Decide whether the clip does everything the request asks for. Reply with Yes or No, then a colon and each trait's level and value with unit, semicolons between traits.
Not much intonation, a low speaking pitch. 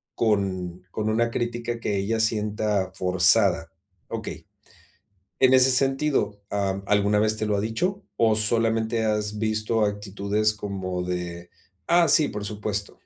Yes: narrow, 2.2 semitones; low, 105 Hz